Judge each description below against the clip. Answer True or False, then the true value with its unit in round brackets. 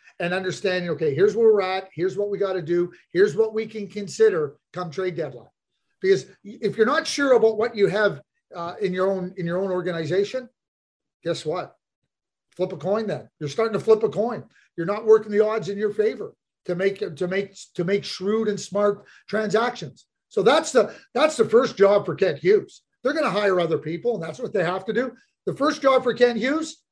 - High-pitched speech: True (205 Hz)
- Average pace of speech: False (215 wpm)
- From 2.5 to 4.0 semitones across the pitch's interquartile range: False (5.1 semitones)